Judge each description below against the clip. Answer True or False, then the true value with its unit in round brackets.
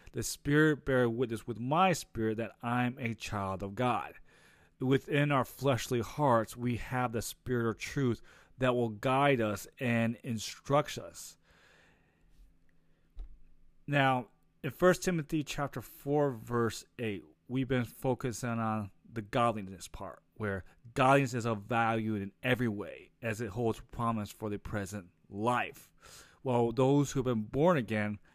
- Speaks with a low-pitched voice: True (120 Hz)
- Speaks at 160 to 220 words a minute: False (145 wpm)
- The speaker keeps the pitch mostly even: False (3.8 semitones)